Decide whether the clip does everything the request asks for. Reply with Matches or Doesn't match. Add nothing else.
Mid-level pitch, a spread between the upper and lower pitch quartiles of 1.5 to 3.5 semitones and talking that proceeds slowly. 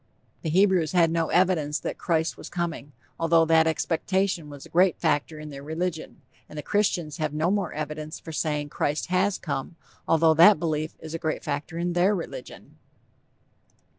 Doesn't match